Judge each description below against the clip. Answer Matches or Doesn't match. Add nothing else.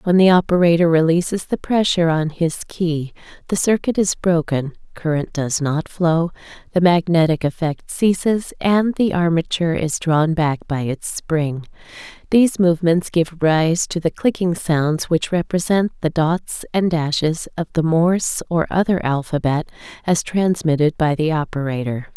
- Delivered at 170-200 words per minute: Doesn't match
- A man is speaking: Doesn't match